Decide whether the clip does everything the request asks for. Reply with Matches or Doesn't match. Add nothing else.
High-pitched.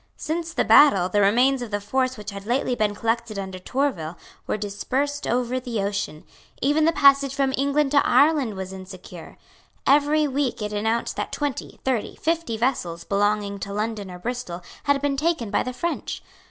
Matches